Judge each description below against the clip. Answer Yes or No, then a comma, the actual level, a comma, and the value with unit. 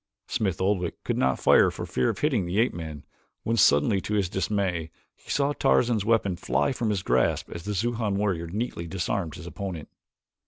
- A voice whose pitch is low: Yes, very low, 95 Hz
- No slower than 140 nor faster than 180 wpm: No, average, 190 wpm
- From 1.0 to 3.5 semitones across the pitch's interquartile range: No, average, 4.3 semitones